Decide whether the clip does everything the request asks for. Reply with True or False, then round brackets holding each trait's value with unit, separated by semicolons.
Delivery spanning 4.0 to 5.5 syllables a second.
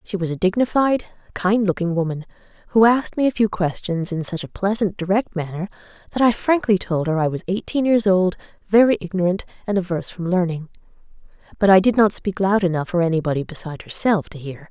False (6.0 syllables/s)